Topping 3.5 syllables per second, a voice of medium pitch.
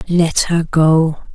No: 3.0 syllables/s; medium, 165 Hz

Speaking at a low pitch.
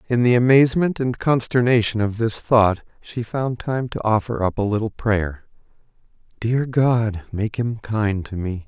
Yes: low, 115 Hz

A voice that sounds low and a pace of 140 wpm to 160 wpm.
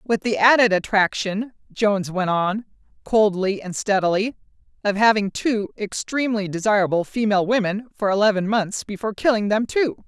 No: high, 210 Hz; average, 145 wpm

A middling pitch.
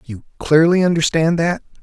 Yes: medium, 160 Hz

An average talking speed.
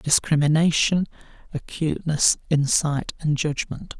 No: slow, 75 wpm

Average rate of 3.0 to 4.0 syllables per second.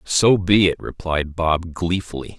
Yes: 3.9 syllables/s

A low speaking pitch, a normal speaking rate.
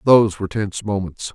Yes: low, 105 Hz; average, 180 wpm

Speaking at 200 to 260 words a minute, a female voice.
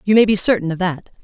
No: fast, 290 wpm; female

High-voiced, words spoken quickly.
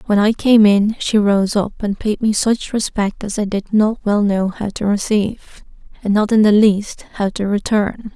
Yes: high, 210 Hz; fast, 215 wpm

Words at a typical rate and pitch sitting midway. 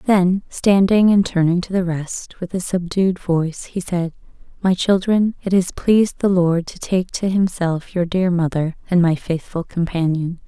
Yes: average, 180 wpm; medium, 180 Hz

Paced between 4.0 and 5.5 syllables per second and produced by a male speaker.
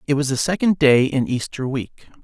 Yes: 5.0 syllables/s; male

